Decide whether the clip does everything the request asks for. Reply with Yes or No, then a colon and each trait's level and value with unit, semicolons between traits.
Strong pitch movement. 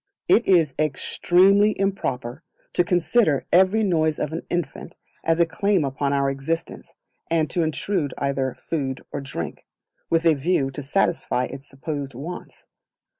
No: average, 4.4 semitones